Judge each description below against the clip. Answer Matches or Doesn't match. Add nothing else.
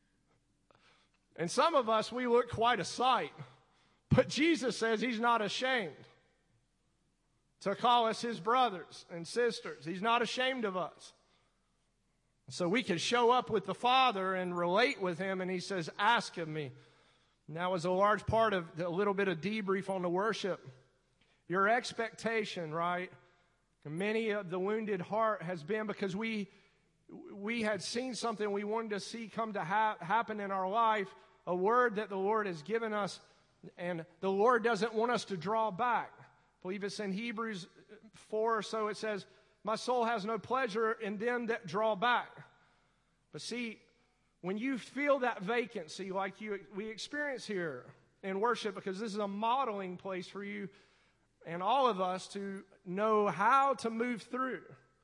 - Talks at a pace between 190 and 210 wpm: Doesn't match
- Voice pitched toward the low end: Doesn't match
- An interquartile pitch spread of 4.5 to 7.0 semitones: Doesn't match